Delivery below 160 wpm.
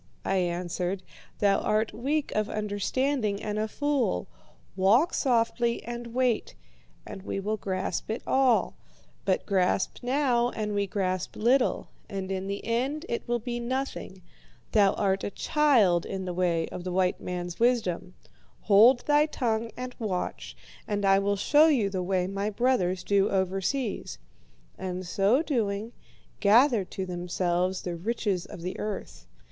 Yes: average, 150 wpm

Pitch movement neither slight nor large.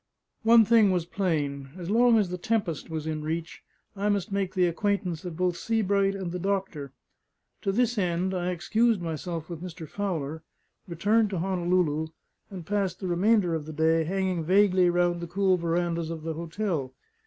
Yes: average, 3.2 semitones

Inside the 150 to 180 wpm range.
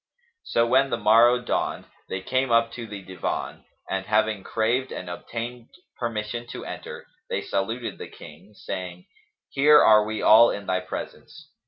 Yes: average, 160 wpm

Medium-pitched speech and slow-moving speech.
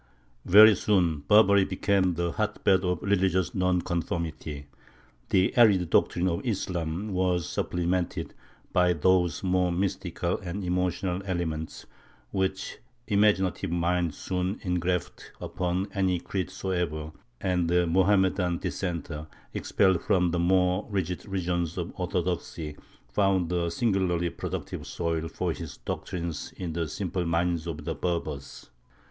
No: very low, 90 Hz; slow, 120 wpm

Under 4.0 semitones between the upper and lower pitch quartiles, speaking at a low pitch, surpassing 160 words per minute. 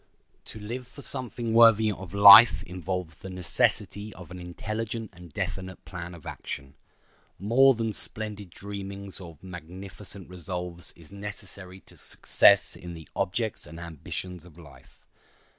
No: average, 3.2 semitones; very low, 95 Hz; average, 140 wpm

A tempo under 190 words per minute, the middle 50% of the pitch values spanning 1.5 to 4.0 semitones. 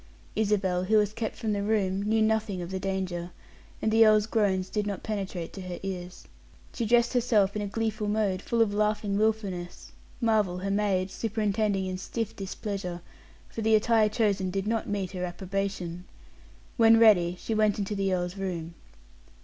Yes: average, 175 wpm; narrow, 2.6 semitones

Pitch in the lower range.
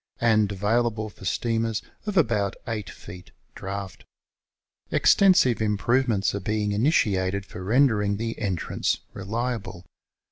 Yes: low, 105 Hz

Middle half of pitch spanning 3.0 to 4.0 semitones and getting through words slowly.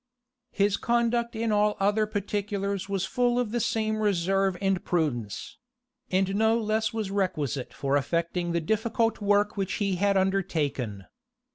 No: average, 3.5 semitones; average, 145 wpm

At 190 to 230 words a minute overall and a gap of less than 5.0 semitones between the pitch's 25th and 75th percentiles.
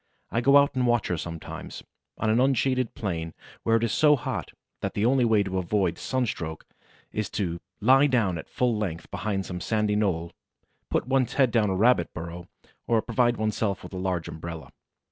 No: average, 195 wpm; wide, 5.4 semitones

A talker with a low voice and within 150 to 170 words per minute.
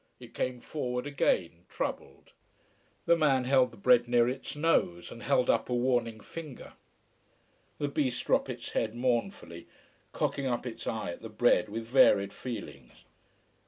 Yes: low, 125 Hz; average, 155 wpm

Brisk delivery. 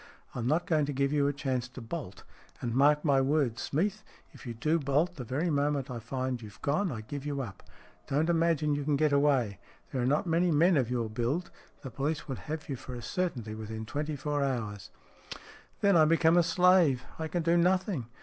Yes: fast, 215 wpm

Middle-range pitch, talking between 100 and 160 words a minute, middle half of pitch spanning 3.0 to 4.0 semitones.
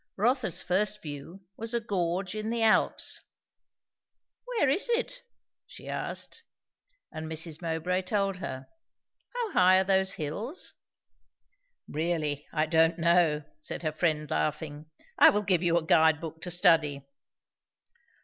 No: medium, 175 Hz; slow, 135 wpm; average, 4.5 semitones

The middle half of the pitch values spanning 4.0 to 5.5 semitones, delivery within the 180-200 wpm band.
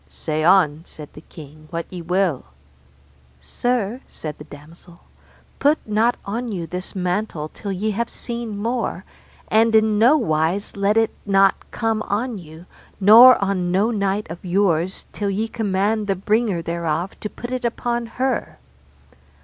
No: average, 4.6 semitones; average, 155 wpm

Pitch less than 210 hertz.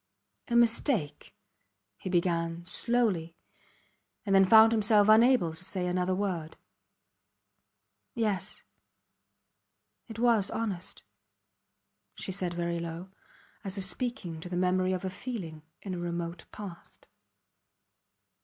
Yes: medium, 185 Hz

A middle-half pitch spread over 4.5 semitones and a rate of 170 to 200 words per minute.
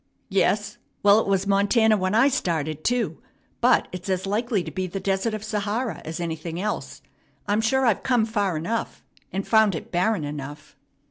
No: average, 3.7 semitones; average, 180 wpm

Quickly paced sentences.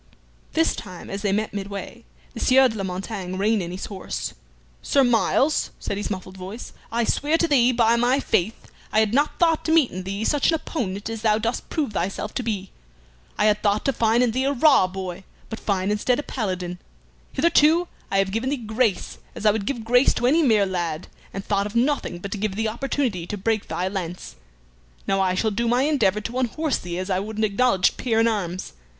Yes: fast, 220 wpm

